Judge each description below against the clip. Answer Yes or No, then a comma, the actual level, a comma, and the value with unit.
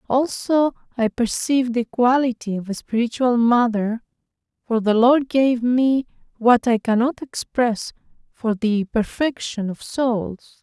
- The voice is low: No, high, 240 Hz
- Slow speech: Yes, slow, 130 wpm